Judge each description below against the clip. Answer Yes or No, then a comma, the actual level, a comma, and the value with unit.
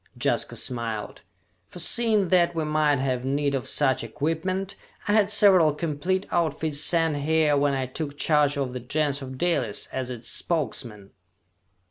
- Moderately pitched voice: Yes, medium, 150 Hz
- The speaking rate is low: No, average, 150 wpm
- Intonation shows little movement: No, average, 4.2 semitones